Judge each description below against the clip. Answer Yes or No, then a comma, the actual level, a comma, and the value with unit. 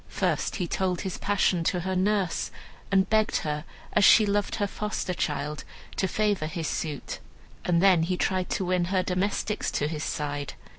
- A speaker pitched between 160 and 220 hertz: Yes, medium, 185 Hz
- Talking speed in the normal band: Yes, average, 180 wpm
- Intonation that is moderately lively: Yes, average, 3.4 semitones